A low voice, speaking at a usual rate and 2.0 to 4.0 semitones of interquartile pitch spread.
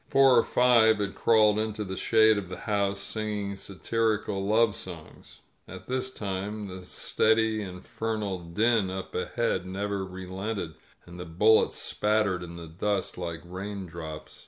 Yes: low, 100 Hz; average, 155 wpm; average, 3.0 semitones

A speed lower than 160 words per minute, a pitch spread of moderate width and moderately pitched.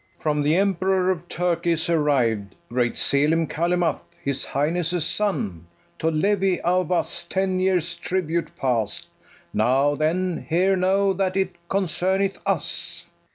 Yes: slow, 135 wpm; average, 4.0 semitones; medium, 170 Hz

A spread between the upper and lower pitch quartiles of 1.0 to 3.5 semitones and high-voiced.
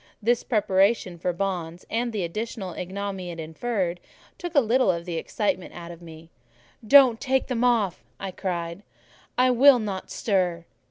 No: average, 5.3 semitones; high, 195 Hz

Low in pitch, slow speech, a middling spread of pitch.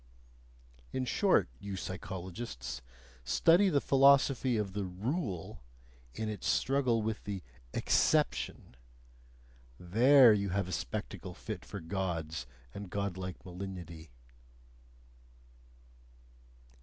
Yes: low, 100 Hz; slow, 95 wpm; average, 4.7 semitones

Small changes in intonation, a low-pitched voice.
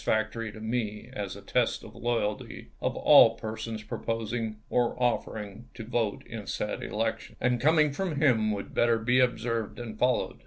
Yes: narrow, 2.1 semitones; low, 115 Hz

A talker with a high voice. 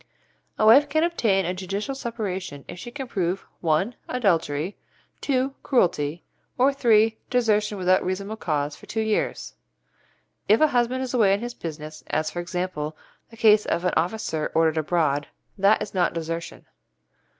Yes: high, 195 Hz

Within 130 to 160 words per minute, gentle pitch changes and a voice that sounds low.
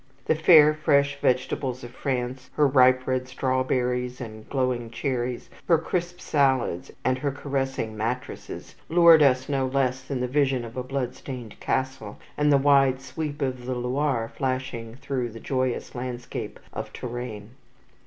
Yes: average, 150 wpm; narrow, 1.9 semitones; low, 130 Hz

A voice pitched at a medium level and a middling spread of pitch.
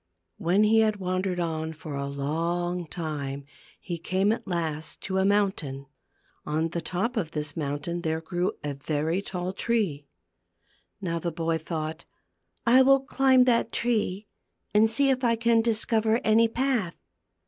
No: medium, 180 Hz; wide, 5.7 semitones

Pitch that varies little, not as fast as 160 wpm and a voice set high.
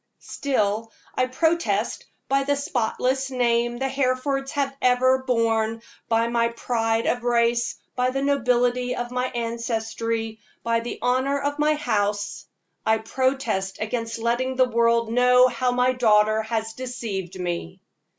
Yes: narrow, 2.3 semitones; average, 140 wpm; high, 240 Hz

